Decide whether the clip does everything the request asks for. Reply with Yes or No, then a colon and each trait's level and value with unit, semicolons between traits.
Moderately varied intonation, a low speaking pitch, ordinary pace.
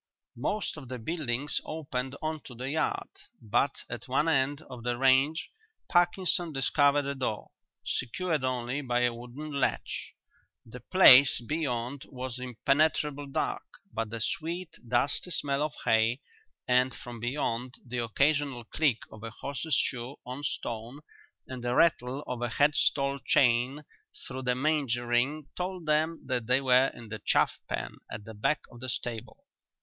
Yes: average, 3.4 semitones; low, 130 Hz; average, 155 wpm